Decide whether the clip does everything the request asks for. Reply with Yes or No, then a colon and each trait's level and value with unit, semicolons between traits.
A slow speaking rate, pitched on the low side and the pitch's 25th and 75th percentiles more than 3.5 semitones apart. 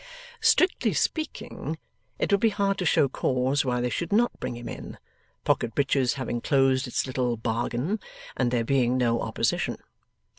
No: average, 160 wpm; low, 130 Hz; average, 5.2 semitones